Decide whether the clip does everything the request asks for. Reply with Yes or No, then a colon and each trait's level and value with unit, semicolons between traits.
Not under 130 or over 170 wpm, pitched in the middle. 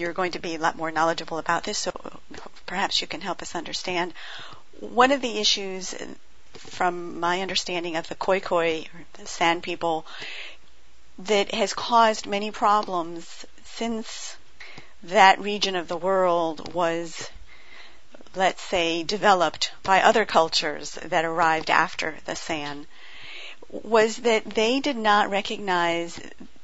Yes: slow, 135 wpm; medium, 180 Hz